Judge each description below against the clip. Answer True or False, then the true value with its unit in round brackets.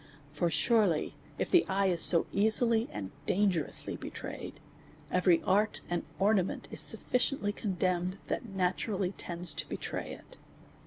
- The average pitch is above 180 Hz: True (190 Hz)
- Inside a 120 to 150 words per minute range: True (140 wpm)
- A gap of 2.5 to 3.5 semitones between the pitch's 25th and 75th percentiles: True (3.2 semitones)